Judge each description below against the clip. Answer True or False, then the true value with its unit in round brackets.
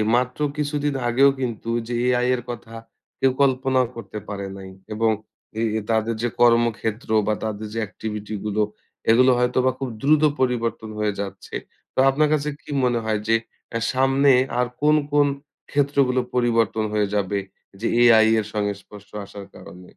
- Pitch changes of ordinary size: True (3.3 semitones)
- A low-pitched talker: True (115 Hz)